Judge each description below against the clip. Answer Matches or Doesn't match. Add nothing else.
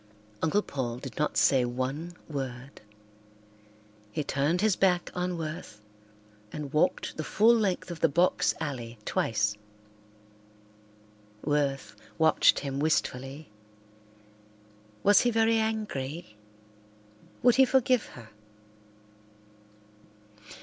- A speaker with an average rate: Doesn't match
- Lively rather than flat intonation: Matches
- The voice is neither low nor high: Matches